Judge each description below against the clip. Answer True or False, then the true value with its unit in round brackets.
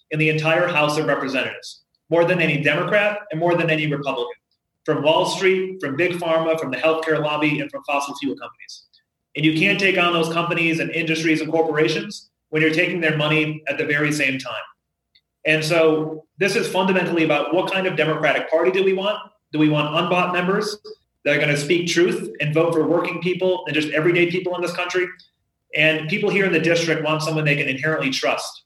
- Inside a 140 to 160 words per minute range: False (205 wpm)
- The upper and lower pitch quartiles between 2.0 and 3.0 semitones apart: True (2.6 semitones)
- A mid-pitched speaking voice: True (160 Hz)